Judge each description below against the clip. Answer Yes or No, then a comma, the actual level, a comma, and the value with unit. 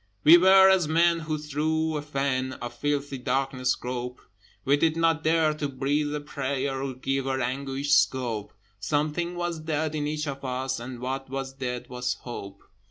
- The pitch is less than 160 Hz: Yes, medium, 140 Hz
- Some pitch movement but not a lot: Yes, average, 3.0 semitones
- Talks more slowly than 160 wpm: No, average, 175 wpm